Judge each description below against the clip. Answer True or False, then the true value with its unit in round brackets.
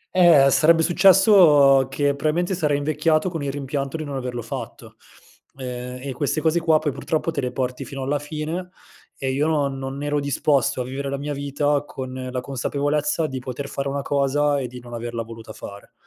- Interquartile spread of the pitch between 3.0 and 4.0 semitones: False (2.6 semitones)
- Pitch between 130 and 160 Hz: True (140 Hz)